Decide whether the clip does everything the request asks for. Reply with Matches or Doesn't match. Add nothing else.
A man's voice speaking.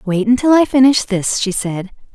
Doesn't match